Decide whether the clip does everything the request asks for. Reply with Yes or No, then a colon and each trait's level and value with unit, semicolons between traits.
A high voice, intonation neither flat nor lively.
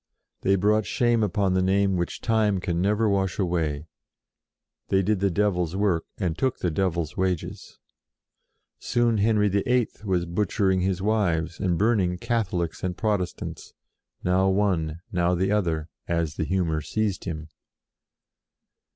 No: very low, 95 Hz; average, 3.2 semitones